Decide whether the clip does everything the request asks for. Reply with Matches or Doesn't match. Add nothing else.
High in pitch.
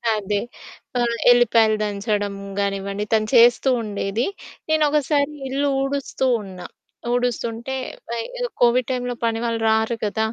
Matches